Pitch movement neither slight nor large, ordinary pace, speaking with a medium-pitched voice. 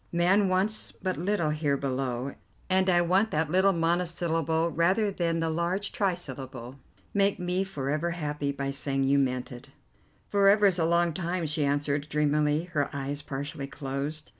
Yes: average, 4.3 semitones; average, 165 wpm; medium, 160 Hz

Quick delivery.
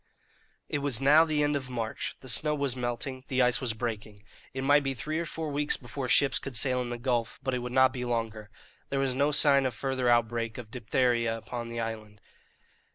Yes: fast, 220 wpm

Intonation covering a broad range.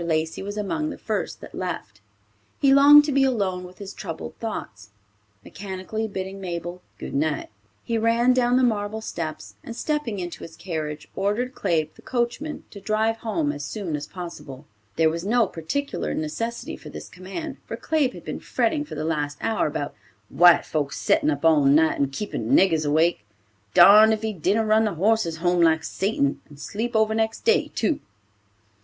Yes: wide, 6.0 semitones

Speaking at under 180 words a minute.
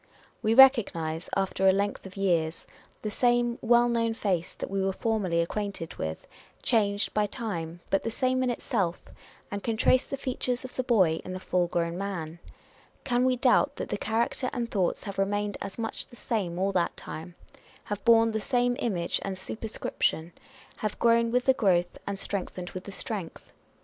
No: average, 185 wpm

